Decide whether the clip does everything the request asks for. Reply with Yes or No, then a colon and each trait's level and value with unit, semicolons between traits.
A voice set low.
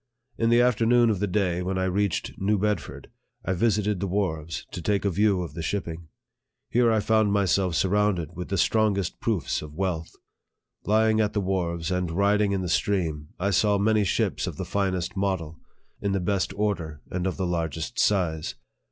Yes: very low, 95 Hz